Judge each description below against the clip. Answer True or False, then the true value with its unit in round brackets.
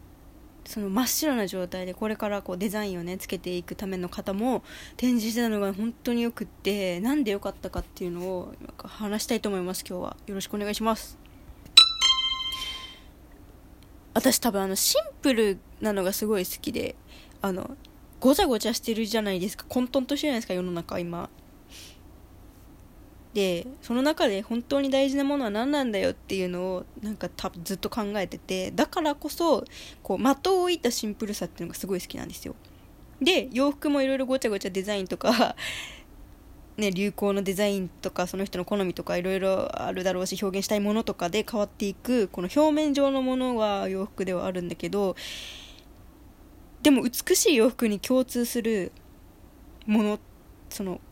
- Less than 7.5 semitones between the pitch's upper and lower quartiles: True (5.1 semitones)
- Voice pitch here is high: True (210 Hz)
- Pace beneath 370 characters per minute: True (355 characters per minute)